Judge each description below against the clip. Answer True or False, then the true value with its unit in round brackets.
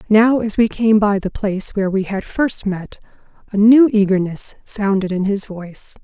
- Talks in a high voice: True (205 Hz)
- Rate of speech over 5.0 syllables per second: False (4.8 syllables/s)